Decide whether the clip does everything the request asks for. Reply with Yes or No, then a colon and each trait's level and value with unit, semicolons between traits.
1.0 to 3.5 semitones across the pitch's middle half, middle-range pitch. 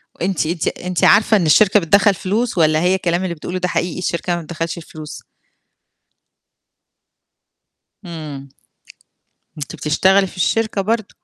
Yes: average, 3.1 semitones; medium, 175 Hz